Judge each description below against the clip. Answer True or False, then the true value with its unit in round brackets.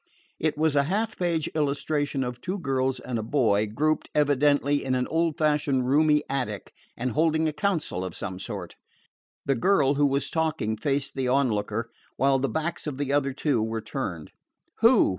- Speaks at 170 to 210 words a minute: True (180 wpm)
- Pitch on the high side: False (140 Hz)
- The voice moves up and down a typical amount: True (3.4 semitones)